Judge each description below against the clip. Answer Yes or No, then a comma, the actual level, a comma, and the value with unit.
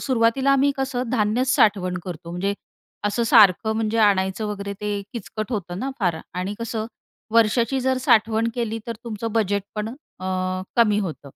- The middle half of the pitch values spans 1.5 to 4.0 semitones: Yes, average, 2.7 semitones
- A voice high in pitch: Yes, high, 220 Hz